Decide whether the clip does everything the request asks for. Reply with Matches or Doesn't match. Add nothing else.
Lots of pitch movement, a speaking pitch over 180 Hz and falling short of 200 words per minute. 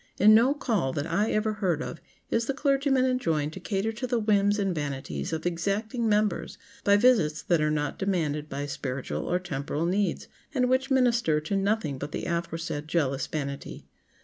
Matches